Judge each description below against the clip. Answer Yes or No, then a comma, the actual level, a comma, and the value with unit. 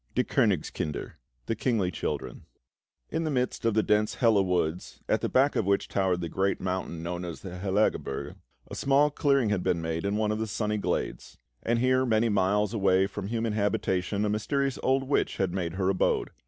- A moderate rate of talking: Yes, average, 195 wpm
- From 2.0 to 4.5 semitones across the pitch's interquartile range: Yes, average, 3.9 semitones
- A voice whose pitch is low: Yes, low, 105 Hz